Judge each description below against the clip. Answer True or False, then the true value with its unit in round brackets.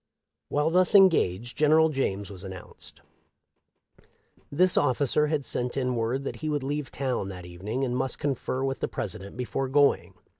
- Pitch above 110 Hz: True (135 Hz)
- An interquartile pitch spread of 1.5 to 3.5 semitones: False (4.2 semitones)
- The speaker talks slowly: False (160 wpm)